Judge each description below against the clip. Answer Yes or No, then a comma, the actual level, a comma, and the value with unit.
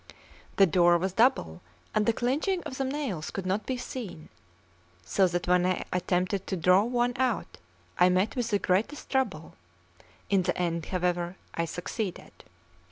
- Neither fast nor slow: Yes, average, 165 wpm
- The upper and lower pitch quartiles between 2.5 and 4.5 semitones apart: No, average, 5.3 semitones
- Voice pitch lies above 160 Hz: Yes, high, 190 Hz